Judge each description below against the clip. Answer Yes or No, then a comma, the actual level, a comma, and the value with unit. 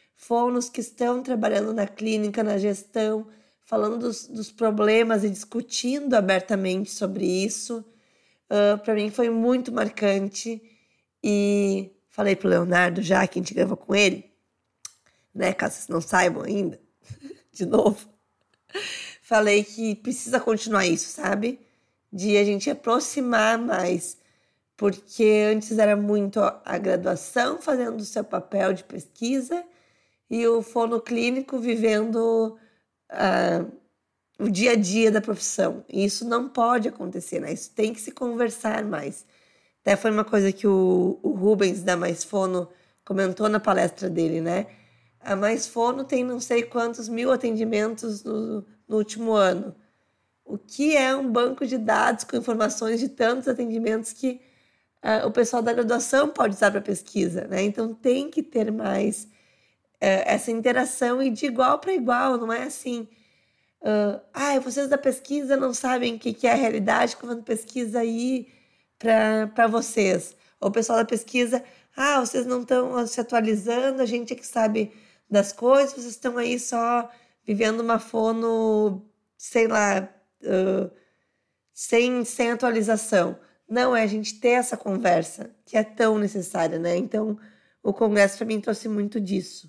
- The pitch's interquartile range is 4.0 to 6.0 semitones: No, average, 3.1 semitones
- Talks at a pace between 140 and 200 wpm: Yes, average, 150 wpm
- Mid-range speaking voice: No, high, 220 Hz